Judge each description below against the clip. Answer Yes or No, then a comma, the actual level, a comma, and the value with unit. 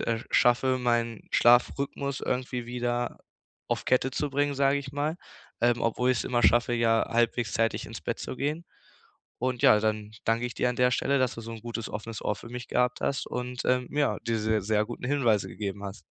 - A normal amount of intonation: No, narrow, 2.1 semitones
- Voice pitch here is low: Yes, low, 120 Hz